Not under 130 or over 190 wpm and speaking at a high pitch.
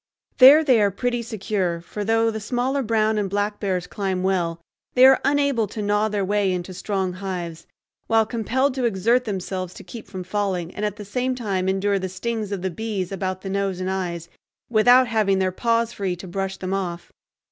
No: average, 200 wpm; high, 205 Hz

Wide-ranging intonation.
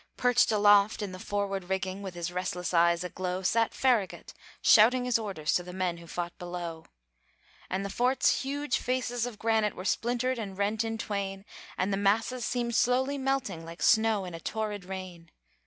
No: average, 4.4 semitones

